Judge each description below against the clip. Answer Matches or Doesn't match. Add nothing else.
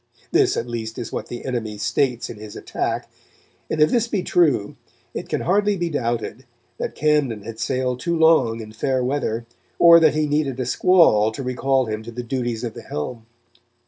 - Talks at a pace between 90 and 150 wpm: Doesn't match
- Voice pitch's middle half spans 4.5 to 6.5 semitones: Matches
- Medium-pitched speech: Doesn't match